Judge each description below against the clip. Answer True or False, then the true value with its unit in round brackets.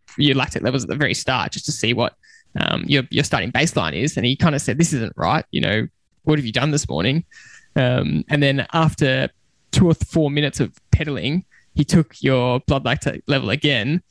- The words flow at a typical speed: False (215 wpm)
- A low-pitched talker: False (145 Hz)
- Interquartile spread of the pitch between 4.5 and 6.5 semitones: False (3.0 semitones)